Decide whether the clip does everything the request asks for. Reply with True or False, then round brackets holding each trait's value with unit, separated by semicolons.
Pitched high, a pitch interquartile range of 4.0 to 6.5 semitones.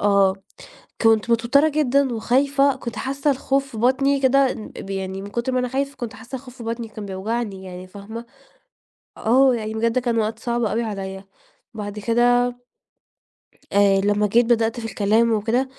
False (230 Hz; 3.5 semitones)